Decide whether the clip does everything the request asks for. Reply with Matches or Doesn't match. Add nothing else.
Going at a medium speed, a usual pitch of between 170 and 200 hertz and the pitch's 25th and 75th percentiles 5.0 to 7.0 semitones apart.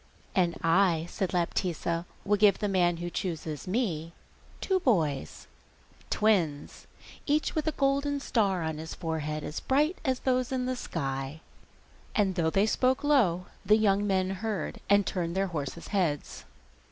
Matches